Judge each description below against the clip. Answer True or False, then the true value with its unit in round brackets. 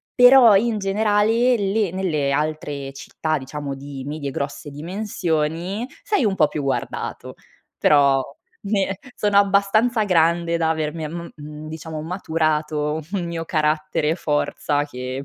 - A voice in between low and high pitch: True (160 Hz)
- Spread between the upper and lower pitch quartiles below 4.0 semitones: False (4.9 semitones)